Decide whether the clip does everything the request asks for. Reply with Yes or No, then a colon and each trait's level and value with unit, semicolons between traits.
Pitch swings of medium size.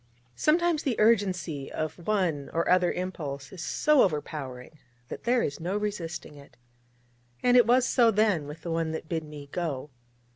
No: wide, 6.0 semitones